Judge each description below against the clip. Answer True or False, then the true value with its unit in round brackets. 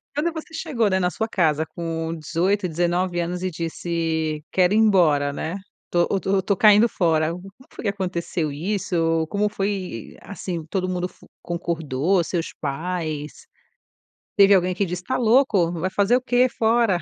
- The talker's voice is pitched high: False (180 Hz)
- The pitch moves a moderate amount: True (3.6 semitones)